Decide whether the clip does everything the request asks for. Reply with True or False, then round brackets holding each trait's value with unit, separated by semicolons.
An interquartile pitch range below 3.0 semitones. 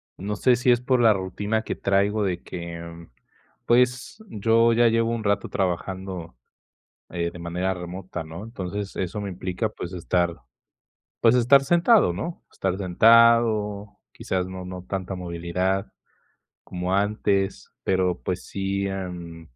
False (3.8 semitones)